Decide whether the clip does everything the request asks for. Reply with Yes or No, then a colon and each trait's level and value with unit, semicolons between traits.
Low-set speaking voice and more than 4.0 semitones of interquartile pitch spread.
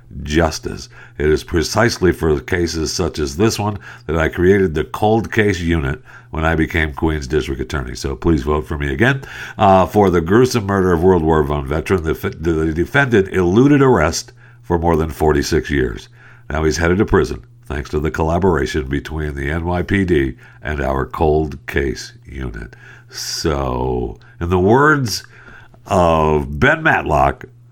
Yes: very low, 85 Hz; average, 4.5 semitones